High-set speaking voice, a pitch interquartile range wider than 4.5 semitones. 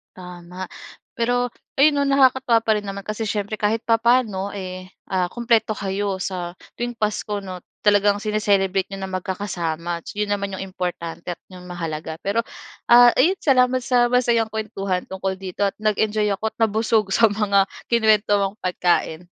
No: high, 205 Hz; average, 3.4 semitones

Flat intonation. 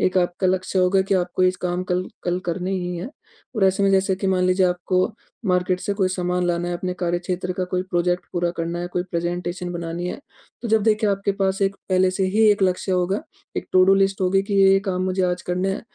Yes: narrow, 1.4 semitones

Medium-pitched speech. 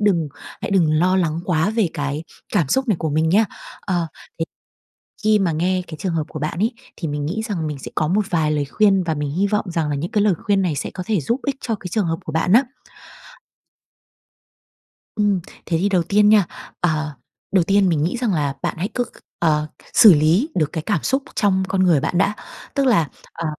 Yes: medium, 180 Hz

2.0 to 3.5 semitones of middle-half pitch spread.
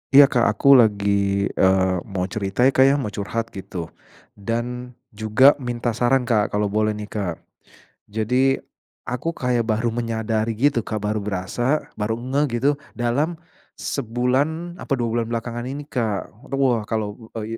Yes: average, 3.2 semitones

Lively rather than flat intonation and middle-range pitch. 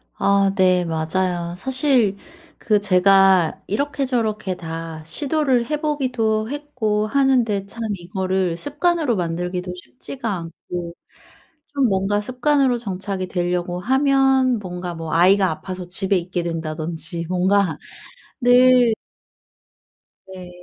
No: wide, 5.8 semitones; high, 195 Hz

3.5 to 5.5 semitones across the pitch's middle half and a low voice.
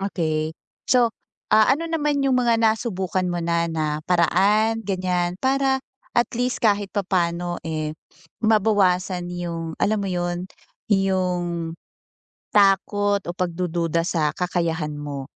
No: average, 4.1 semitones; medium, 185 Hz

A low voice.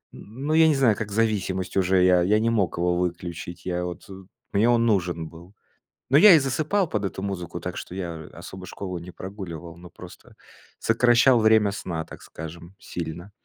Yes: very low, 95 Hz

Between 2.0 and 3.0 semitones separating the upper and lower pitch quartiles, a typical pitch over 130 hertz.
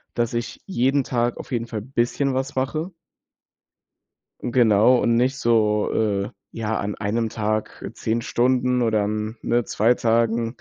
No: narrow, 2.5 semitones; low, 115 Hz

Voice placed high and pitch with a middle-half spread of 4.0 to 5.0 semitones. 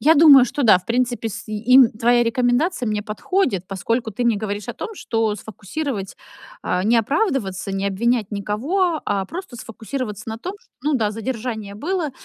Yes: high, 230 Hz; average, 4.7 semitones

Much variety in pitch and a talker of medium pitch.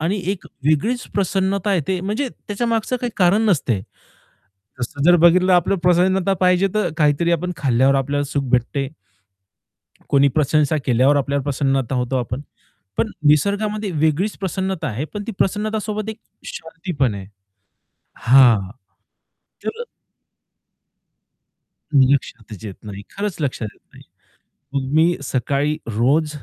Yes: wide, 6.2 semitones; medium, 155 Hz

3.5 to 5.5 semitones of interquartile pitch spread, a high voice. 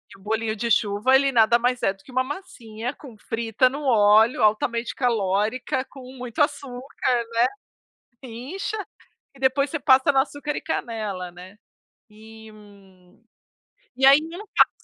Yes: average, 3.8 semitones; high, 235 Hz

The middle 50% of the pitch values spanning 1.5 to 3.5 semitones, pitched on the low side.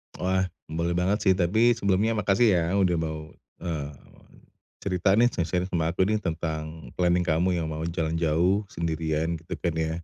Yes: average, 2.7 semitones; very low, 85 Hz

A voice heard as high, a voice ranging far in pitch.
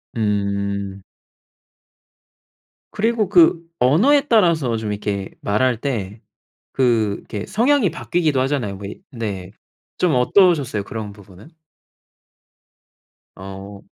No: low, 115 Hz; wide, 8.6 semitones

